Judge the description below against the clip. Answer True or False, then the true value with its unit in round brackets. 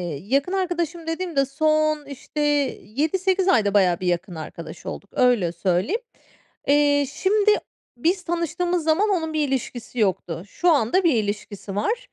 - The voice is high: True (290 Hz)